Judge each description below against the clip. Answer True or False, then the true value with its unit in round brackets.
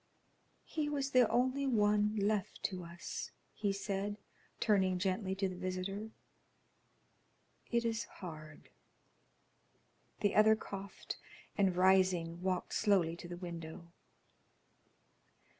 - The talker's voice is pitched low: False (195 Hz)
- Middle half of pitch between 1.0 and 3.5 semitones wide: True (2.8 semitones)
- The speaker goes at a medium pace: False (110 wpm)